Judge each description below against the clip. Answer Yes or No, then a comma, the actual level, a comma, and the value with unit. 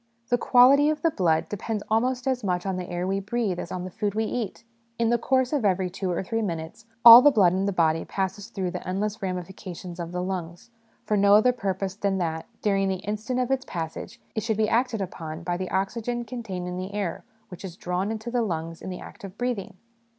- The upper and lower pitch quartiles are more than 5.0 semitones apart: No, average, 4.1 semitones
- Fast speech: Yes, fast, 230 wpm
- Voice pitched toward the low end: No, high, 195 Hz